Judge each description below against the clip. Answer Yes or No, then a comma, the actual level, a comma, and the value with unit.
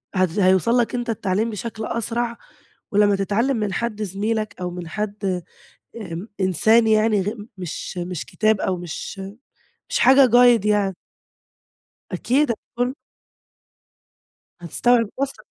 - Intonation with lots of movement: No, average, 3.7 semitones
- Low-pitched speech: No, high, 215 Hz